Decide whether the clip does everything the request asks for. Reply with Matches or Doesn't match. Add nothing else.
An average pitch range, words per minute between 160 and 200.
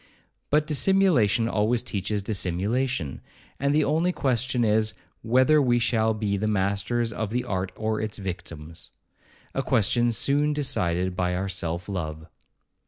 Doesn't match